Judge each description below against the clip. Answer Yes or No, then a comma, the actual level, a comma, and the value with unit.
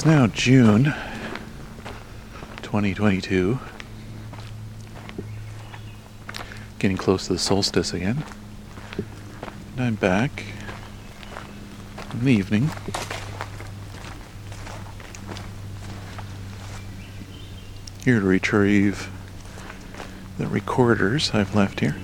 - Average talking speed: No, slow, 65 wpm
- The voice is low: Yes, low, 100 Hz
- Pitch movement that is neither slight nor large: No, narrow, 1.6 semitones